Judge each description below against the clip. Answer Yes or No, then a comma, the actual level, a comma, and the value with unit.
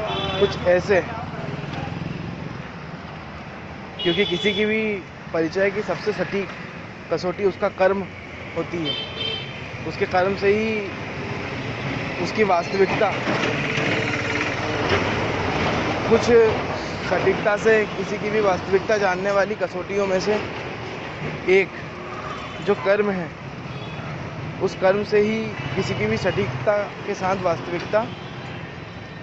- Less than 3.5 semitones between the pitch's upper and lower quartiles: No, average, 4.1 semitones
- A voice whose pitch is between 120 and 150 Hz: No, medium, 180 Hz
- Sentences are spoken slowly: Yes, slow, 100 wpm